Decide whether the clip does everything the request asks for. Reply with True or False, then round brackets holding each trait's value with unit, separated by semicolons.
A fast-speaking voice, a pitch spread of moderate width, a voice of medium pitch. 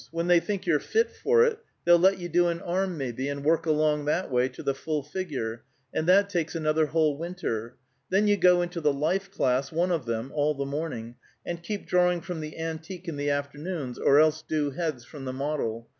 True (220 wpm; 3.8 semitones; 155 Hz)